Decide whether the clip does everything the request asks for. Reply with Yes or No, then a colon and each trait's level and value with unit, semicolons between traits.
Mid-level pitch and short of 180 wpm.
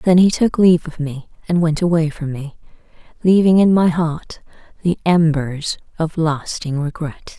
Yes: medium, 165 Hz; average, 160 wpm